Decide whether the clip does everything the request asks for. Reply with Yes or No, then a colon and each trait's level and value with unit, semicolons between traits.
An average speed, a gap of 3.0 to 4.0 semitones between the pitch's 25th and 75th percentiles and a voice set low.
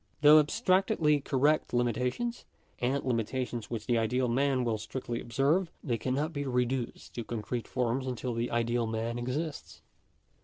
Yes: average, 145 wpm; average, 3.3 semitones; low, 125 Hz